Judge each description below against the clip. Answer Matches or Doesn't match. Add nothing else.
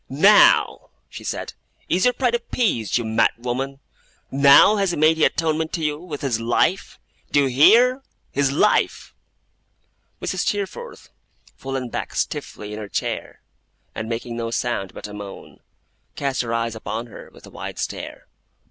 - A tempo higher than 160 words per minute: Doesn't match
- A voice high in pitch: Doesn't match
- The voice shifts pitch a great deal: Matches